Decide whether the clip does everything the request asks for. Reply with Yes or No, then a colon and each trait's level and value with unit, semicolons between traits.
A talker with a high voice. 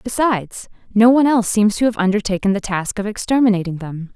Yes: high, 210 Hz